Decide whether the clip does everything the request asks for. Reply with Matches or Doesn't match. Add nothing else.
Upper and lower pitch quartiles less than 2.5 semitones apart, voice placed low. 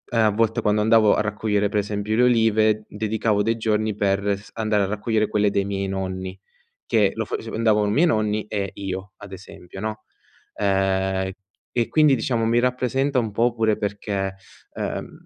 Matches